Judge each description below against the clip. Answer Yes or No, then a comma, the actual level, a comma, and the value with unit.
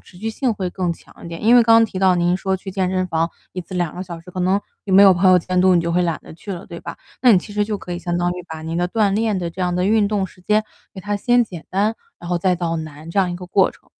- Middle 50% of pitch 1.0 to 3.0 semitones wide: Yes, narrow, 2.6 semitones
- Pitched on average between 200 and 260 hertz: No, medium, 185 Hz